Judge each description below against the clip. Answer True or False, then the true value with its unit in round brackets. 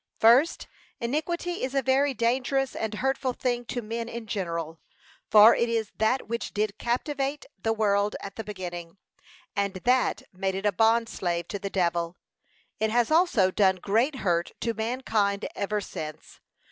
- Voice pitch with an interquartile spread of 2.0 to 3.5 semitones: False (4.1 semitones)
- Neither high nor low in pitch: False (220 Hz)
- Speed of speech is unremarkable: True (160 wpm)